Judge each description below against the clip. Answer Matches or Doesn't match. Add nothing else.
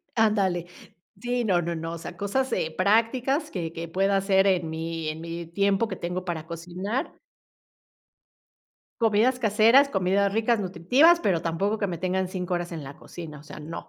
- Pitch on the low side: Doesn't match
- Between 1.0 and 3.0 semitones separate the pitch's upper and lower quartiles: Doesn't match